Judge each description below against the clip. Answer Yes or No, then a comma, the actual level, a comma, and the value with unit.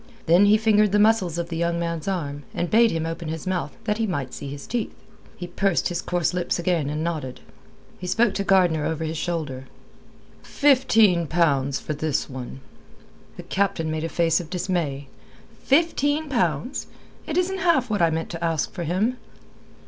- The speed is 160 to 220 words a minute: Yes, average, 185 wpm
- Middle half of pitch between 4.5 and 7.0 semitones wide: Yes, average, 4.8 semitones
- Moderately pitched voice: Yes, medium, 170 Hz